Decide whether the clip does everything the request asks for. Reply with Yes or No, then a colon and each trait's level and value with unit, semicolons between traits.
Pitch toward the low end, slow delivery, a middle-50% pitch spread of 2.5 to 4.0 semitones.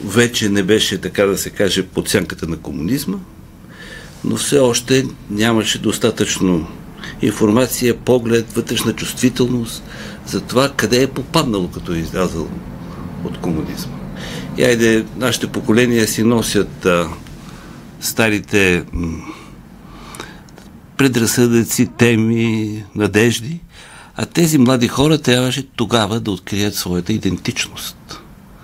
Yes: low, 115 Hz; slow, 110 wpm; average, 3.3 semitones